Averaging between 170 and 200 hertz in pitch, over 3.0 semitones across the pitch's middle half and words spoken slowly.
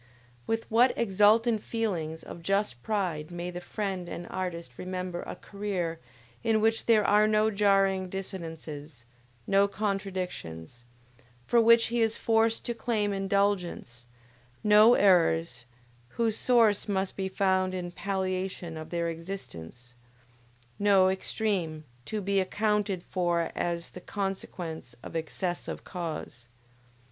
Yes: high, 190 Hz; average, 3.6 semitones; slow, 125 wpm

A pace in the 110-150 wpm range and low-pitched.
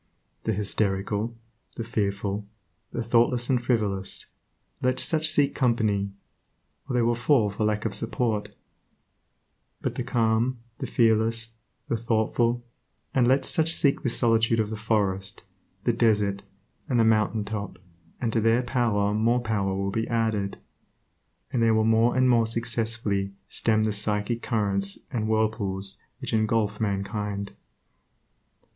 Yes: average, 140 wpm; low, 110 Hz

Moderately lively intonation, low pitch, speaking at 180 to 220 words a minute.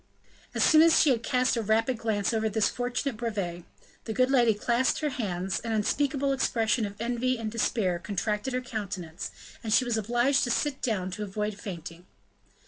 No: average, 3.5 semitones; high, 225 Hz; average, 185 wpm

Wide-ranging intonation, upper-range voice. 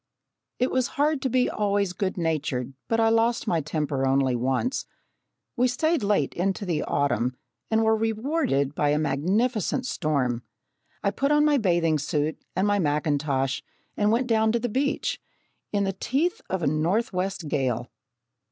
Yes: wide, 7.9 semitones; high, 195 Hz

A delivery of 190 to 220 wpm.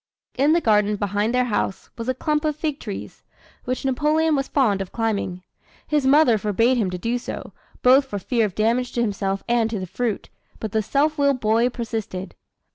Yes: average, 200 wpm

